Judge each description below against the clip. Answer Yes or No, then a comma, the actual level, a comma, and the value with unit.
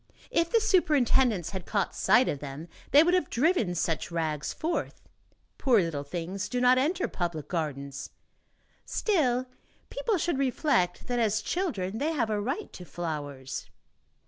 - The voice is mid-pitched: No, high, 220 Hz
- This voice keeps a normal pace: Yes, average, 150 wpm